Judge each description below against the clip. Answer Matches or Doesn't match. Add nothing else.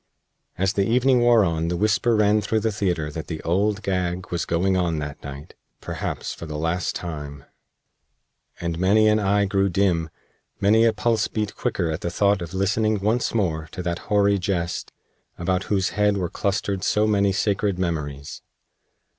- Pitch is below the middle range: Matches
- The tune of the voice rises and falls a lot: Doesn't match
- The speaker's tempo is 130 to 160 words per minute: Doesn't match